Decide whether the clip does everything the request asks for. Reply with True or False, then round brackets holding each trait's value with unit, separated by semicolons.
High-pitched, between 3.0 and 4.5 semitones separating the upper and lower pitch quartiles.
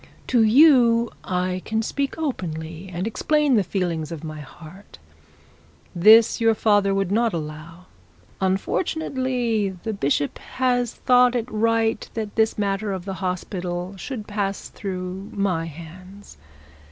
True (200 Hz; 4.0 semitones)